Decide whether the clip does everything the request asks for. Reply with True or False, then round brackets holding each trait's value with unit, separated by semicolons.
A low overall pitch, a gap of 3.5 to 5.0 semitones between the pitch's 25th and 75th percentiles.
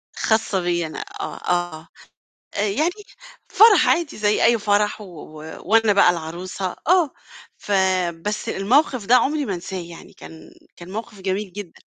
False (195 Hz; 4.2 semitones)